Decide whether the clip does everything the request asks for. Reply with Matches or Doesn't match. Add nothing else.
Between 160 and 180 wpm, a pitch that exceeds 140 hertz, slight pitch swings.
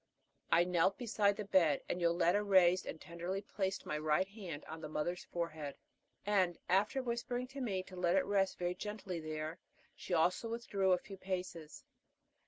Doesn't match